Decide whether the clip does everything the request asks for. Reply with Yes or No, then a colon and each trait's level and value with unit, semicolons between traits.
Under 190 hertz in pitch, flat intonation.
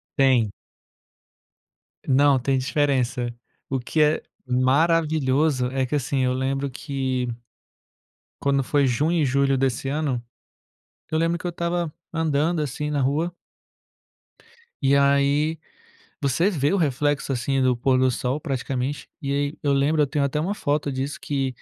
Yes: medium, 140 Hz; narrow, 2.3 semitones